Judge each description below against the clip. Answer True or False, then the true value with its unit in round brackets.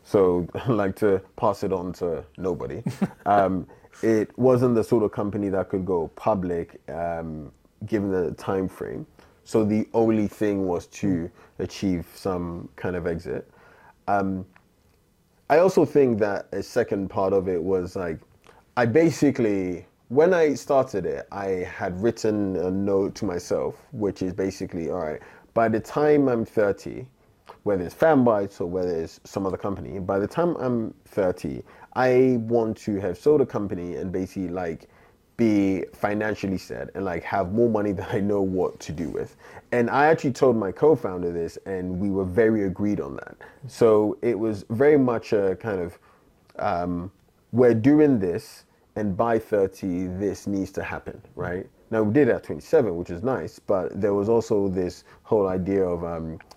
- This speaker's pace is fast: False (170 wpm)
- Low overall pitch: True (100 Hz)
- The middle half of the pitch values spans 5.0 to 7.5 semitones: False (3.4 semitones)